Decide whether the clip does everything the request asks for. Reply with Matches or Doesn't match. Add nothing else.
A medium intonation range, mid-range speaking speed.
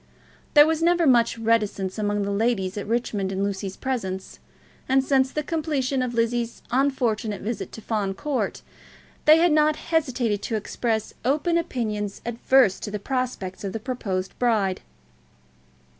Matches